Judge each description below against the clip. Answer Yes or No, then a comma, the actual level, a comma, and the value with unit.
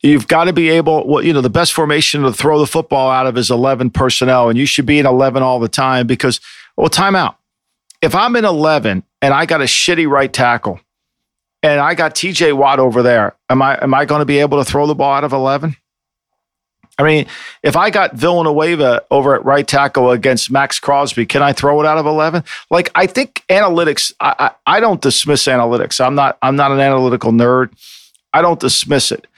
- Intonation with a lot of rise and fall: No, average, 2.9 semitones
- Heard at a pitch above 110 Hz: Yes, medium, 140 Hz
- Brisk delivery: Yes, fast, 220 wpm